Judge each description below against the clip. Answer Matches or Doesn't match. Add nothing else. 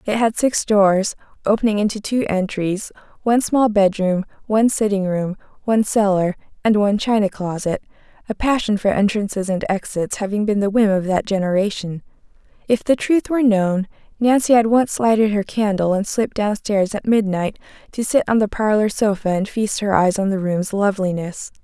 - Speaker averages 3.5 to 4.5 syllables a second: Doesn't match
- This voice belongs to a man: Doesn't match